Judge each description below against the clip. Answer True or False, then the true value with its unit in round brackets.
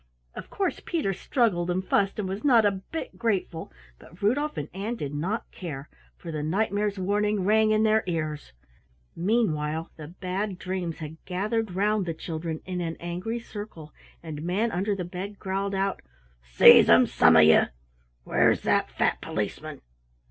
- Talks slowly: False (160 wpm)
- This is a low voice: False (190 Hz)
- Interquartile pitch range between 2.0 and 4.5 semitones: True (4.2 semitones)